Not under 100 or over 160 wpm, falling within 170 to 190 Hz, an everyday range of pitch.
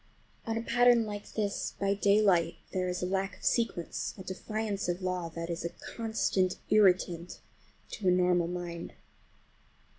Yes: average, 155 wpm; medium, 185 Hz; average, 3.0 semitones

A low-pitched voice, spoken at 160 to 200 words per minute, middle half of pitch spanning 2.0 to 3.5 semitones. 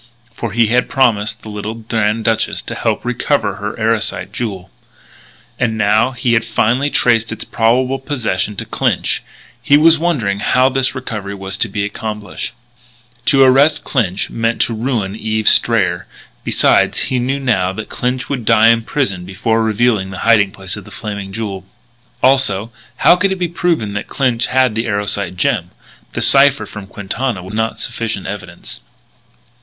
No: low, 115 Hz; average, 170 wpm; average, 3.9 semitones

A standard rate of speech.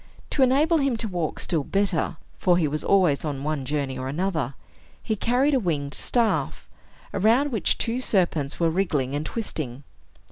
Yes: average, 170 wpm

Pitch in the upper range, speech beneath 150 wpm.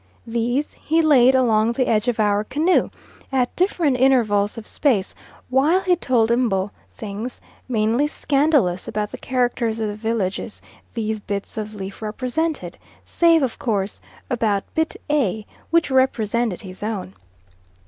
Yes: high, 235 Hz; average, 140 wpm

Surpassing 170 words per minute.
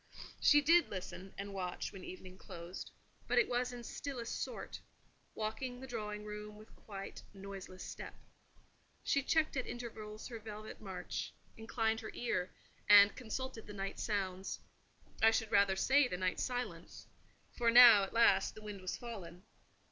No: average, 155 wpm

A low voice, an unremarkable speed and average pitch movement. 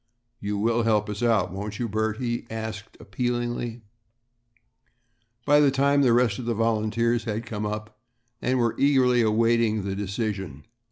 No: low, 115 Hz; average, 155 wpm; narrow, 2.2 semitones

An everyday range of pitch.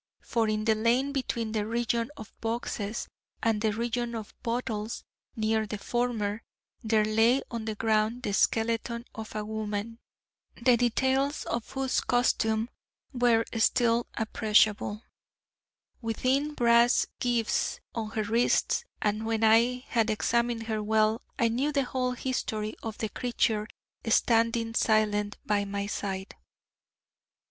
No: narrow, 1.8 semitones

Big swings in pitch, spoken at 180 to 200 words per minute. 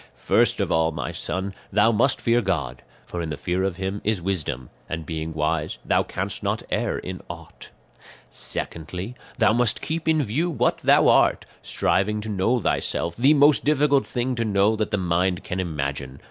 Yes: wide, 6.4 semitones; average, 185 wpm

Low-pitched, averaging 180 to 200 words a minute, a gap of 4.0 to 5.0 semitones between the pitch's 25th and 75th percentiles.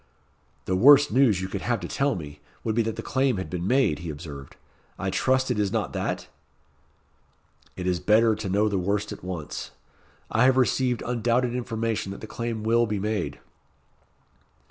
Yes: low, 110 Hz; average, 185 wpm; average, 4.6 semitones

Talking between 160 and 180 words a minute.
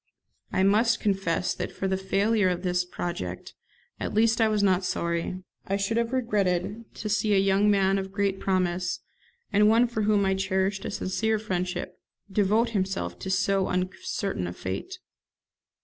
Yes: average, 165 wpm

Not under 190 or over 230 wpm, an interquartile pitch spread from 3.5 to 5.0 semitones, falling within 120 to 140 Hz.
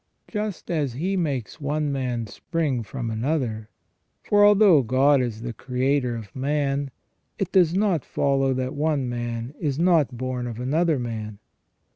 No: average, 150 wpm; average, 4.5 semitones; low, 135 Hz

